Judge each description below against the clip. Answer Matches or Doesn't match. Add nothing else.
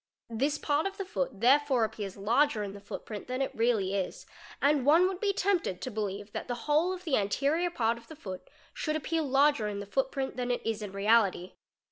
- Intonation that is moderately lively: Doesn't match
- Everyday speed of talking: Doesn't match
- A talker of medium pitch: Doesn't match